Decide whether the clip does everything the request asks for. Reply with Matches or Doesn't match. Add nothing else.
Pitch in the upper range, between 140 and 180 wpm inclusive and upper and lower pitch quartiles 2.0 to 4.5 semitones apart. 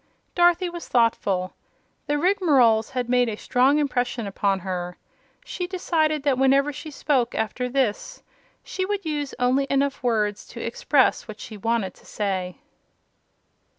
Doesn't match